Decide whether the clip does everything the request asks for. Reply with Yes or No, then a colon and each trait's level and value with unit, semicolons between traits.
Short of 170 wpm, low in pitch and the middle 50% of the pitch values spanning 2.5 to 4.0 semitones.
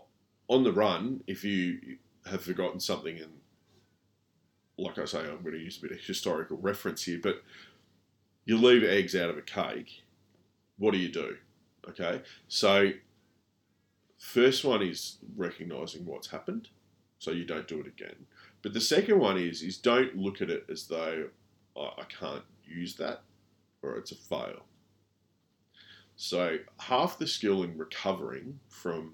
Yes: average, 155 wpm; low, 100 Hz; average, 3.7 semitones